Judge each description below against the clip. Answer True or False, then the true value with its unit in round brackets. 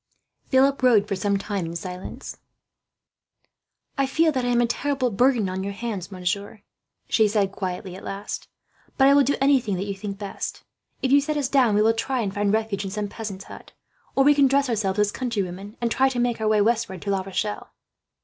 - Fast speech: True (215 wpm)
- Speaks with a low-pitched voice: False (215 Hz)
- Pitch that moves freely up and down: False (4.5 semitones)